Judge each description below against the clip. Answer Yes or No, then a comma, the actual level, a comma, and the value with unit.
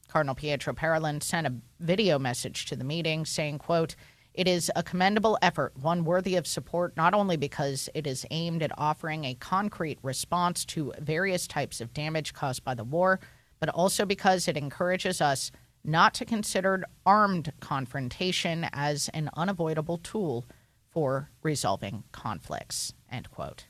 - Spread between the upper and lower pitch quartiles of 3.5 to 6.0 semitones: Yes, average, 4.6 semitones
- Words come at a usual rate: Yes, average, 155 wpm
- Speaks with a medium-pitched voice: Yes, medium, 155 Hz